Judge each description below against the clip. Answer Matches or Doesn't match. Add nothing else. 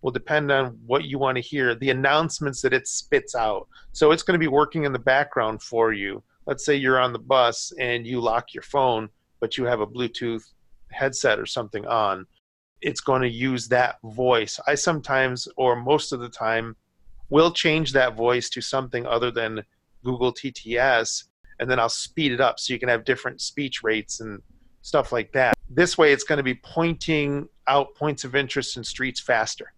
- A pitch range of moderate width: Matches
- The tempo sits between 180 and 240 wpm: Matches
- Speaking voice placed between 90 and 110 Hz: Doesn't match